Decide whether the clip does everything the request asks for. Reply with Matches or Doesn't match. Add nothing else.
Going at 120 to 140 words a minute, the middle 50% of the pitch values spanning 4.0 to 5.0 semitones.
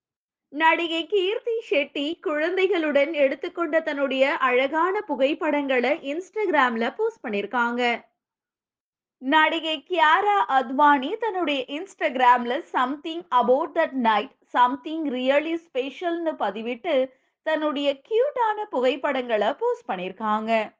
Doesn't match